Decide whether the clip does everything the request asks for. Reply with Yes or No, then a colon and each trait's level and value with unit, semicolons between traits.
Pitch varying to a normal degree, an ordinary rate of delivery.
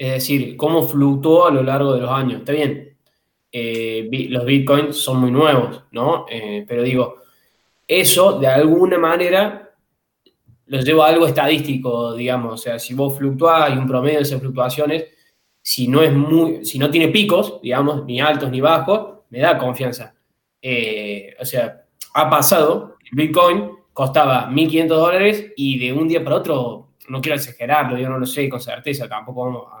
Yes: average, 3.9 semitones; average, 175 wpm